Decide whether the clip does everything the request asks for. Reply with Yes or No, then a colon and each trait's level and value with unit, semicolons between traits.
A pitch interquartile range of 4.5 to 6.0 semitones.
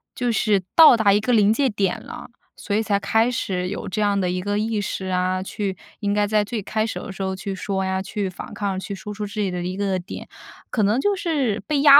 No: narrow, 2.5 semitones